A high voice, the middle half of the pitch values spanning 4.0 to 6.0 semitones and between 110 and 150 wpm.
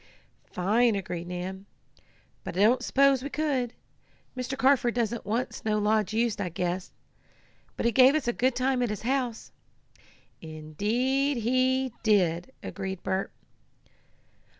Yes: high, 235 Hz; average, 5.0 semitones; slow, 135 wpm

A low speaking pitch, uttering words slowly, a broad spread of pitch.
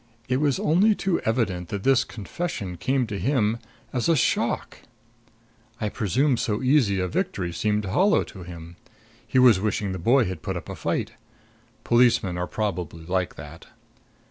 No: low, 105 Hz; average, 165 wpm; wide, 5.9 semitones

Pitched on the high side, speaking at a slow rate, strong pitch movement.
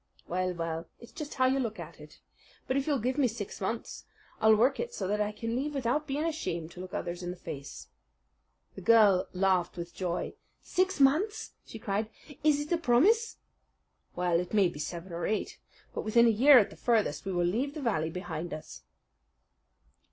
No: high, 215 Hz; average, 200 wpm; wide, 7.3 semitones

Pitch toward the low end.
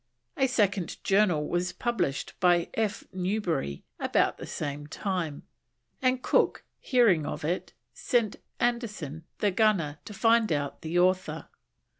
No: medium, 185 Hz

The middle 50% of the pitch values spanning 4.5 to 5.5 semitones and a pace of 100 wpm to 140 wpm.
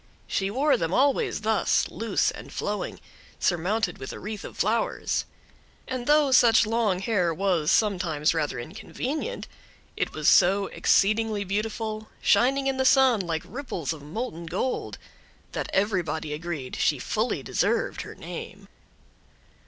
Yes: average, 5.2 semitones; slow, 135 wpm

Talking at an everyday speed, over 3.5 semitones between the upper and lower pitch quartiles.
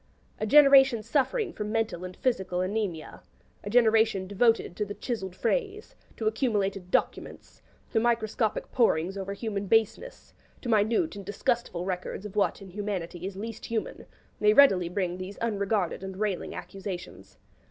No: average, 150 wpm; average, 3.2 semitones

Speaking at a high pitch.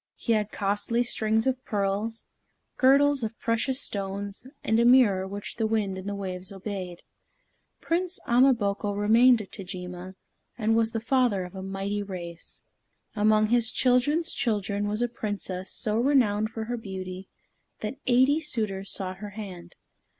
Yes: high, 215 Hz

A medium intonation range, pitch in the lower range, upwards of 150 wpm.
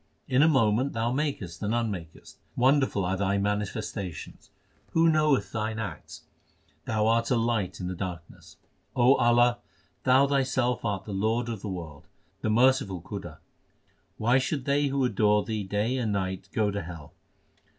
Yes: average, 4.4 semitones; low, 110 Hz; average, 160 wpm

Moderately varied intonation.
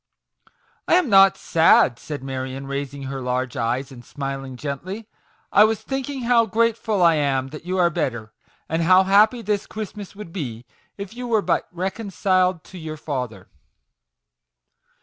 No: wide, 7.3 semitones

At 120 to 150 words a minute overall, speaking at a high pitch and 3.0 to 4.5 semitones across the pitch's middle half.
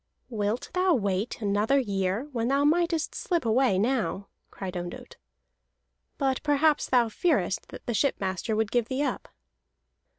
No: average, 140 wpm; high, 235 Hz; wide, 5.6 semitones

